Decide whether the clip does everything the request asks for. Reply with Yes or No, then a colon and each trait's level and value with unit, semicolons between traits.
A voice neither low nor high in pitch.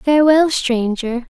No: very high, 265 Hz